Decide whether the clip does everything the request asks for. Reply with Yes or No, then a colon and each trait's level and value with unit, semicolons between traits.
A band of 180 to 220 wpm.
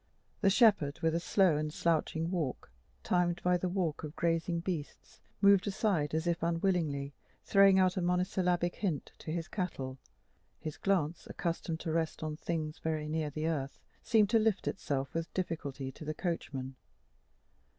No: average, 160 wpm